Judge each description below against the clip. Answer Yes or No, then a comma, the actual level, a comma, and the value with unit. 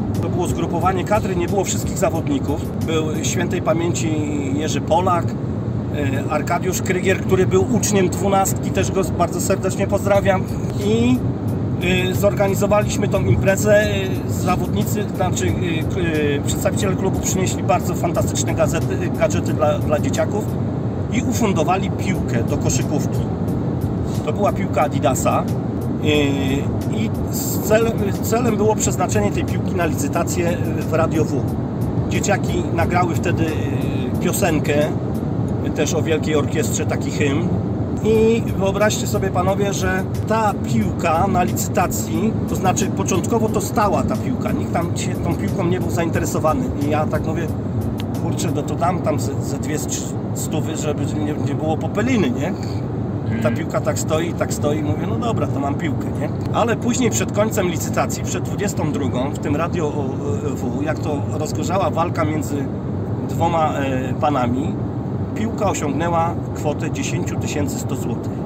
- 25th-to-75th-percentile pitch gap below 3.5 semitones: No, average, 4.2 semitones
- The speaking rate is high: No, average, 125 wpm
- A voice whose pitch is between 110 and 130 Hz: Yes, low, 120 Hz